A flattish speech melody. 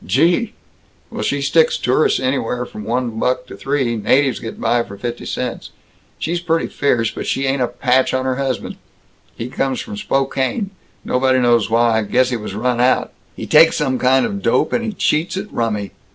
No: average, 3.1 semitones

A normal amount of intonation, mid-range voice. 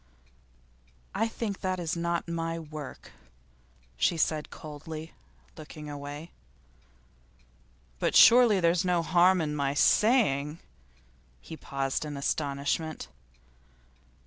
Yes: average, 3.1 semitones; medium, 160 Hz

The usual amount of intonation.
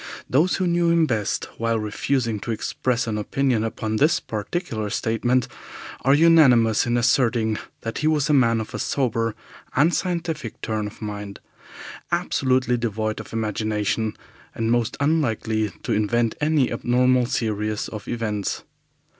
Yes: average, 3.9 semitones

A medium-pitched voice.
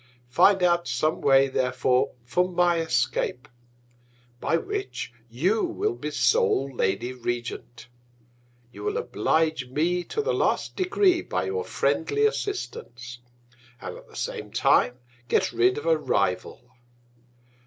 Yes: medium, 155 Hz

